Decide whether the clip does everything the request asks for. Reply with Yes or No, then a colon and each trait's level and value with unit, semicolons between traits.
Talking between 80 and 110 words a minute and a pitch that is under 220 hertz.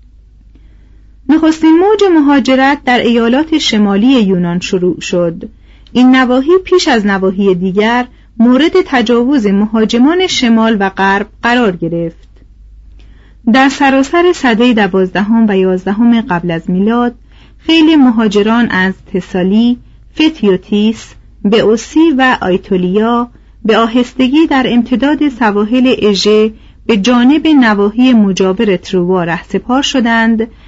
No: slow, 105 wpm; high, 225 Hz